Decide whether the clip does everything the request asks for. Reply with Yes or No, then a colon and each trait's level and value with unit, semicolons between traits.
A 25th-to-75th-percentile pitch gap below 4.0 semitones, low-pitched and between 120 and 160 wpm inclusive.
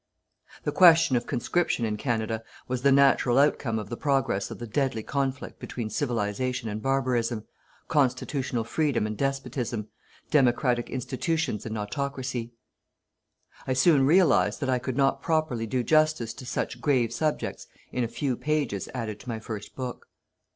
Yes: average, 3.3 semitones; low, 125 Hz; average, 150 wpm